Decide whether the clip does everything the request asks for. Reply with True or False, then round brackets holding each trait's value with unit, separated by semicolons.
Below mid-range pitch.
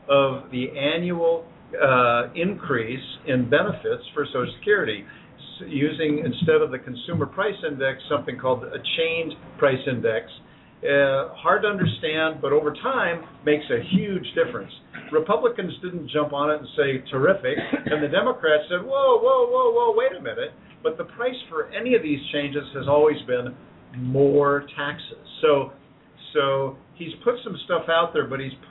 False (150 Hz)